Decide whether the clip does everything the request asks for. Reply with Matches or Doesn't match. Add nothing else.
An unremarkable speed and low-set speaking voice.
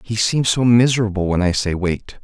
Doesn't match